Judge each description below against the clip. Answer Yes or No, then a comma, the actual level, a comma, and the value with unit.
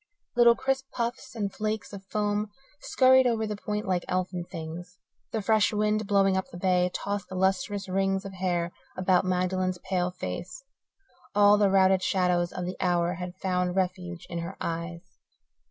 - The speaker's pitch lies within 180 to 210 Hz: Yes, high, 190 Hz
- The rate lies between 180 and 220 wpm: No, average, 170 wpm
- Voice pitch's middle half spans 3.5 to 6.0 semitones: No, narrow, 2.5 semitones